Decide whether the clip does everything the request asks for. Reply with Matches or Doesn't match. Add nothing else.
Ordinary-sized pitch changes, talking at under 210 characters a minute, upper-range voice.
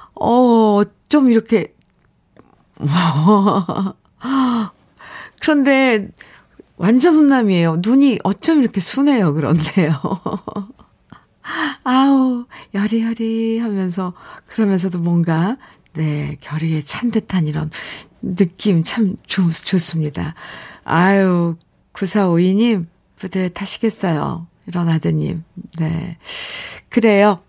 Matches